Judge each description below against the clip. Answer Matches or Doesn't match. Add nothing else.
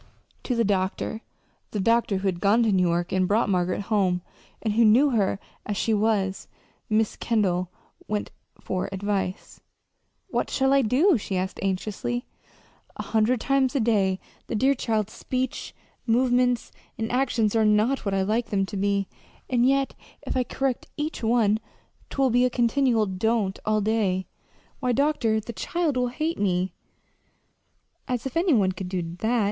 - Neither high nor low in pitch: Doesn't match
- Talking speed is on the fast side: Doesn't match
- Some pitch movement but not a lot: Matches